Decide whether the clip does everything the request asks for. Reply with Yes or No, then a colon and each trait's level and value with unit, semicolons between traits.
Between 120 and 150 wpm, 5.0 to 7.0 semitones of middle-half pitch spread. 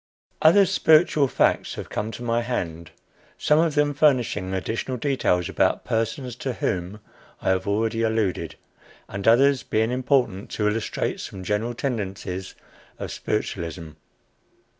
Yes: slow, 135 wpm; average, 5.3 semitones